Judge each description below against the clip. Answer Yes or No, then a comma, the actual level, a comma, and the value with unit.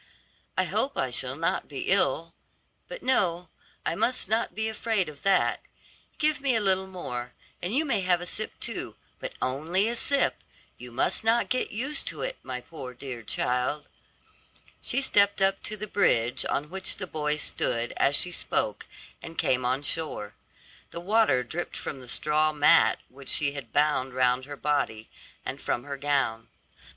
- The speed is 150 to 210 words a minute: Yes, average, 175 wpm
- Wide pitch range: Yes, wide, 7.6 semitones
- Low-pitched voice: No, medium, 155 Hz